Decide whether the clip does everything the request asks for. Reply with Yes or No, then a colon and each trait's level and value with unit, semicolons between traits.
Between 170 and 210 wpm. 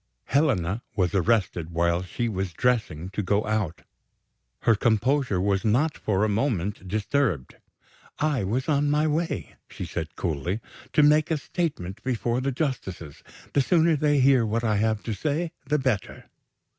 No: average, 155 wpm